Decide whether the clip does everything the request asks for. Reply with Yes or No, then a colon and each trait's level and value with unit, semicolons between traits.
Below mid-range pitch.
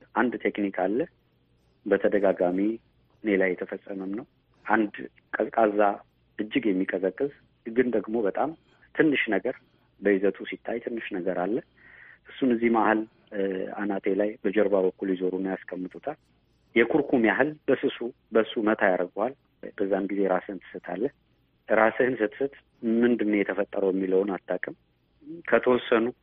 Yes: low, 105 Hz